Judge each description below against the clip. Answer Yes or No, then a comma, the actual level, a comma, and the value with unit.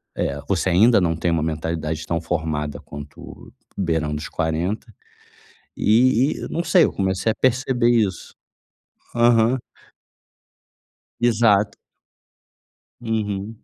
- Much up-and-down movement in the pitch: Yes, wide, 6.1 semitones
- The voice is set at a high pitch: No, very low, 95 Hz